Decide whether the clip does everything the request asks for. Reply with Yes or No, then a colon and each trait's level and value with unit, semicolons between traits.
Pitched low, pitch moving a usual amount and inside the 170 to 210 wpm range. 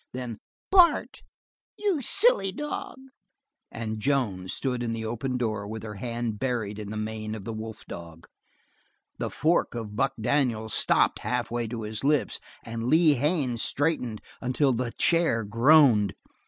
No: low, 120 Hz; average, 4.6 semitones; average, 150 wpm